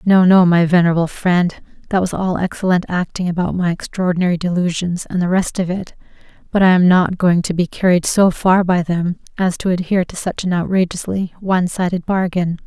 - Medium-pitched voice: Yes, medium, 180 Hz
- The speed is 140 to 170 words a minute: No, average, 195 wpm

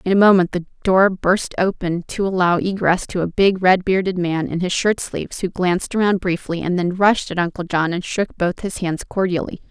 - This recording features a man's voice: No, female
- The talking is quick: Yes, fast, 215 wpm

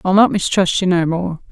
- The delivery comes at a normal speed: No, fast, 235 wpm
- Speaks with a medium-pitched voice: Yes, medium, 180 Hz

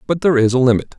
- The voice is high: No, low, 135 Hz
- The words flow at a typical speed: No, fast, 305 wpm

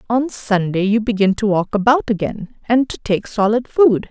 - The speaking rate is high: No, average, 175 wpm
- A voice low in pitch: No, high, 220 Hz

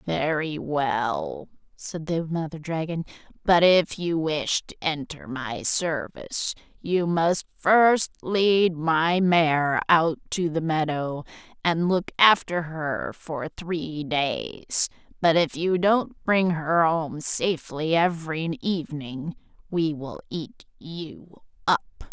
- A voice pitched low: No, medium, 160 Hz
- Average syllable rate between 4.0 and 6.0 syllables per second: No, 3.2 syllables/s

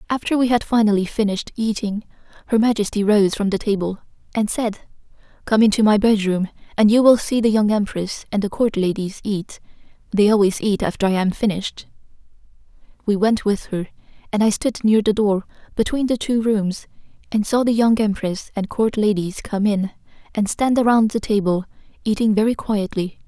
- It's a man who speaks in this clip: No, female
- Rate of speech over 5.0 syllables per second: Yes, 5.3 syllables/s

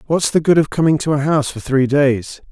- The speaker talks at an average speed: No, fast, 265 wpm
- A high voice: No, medium, 145 Hz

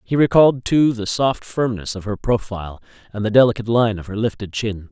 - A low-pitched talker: Yes, low, 110 Hz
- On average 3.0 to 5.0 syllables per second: No, 5.8 syllables/s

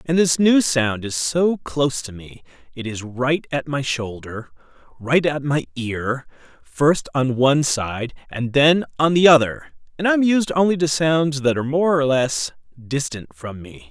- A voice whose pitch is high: No, medium, 140 Hz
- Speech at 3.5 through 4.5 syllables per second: Yes, 4.3 syllables/s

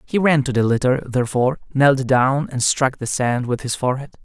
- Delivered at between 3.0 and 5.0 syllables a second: No, 5.5 syllables/s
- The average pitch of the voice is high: No, low, 130 Hz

